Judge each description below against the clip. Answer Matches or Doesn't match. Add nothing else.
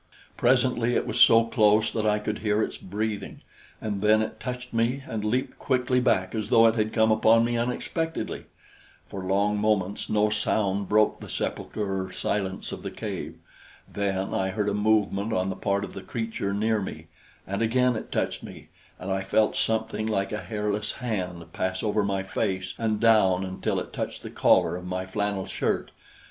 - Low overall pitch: Matches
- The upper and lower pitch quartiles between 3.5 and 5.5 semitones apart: Doesn't match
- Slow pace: Doesn't match